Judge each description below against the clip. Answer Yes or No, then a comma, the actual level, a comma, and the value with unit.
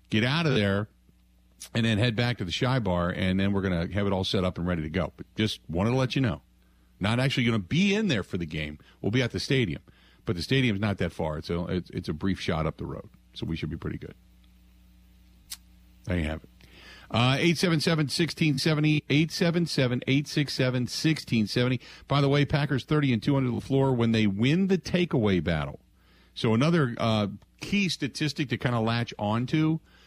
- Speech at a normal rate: No, fast, 210 wpm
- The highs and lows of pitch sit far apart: Yes, wide, 7.9 semitones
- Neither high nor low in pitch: No, low, 115 Hz